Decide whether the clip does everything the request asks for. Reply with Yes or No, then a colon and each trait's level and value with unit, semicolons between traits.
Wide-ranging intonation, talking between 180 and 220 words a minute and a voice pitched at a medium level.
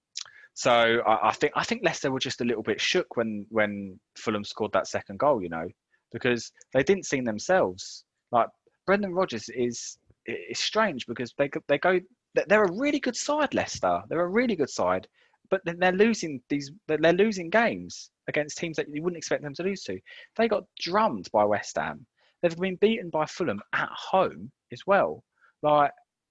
Yes: wide, 8.9 semitones; average, 185 wpm; medium, 165 Hz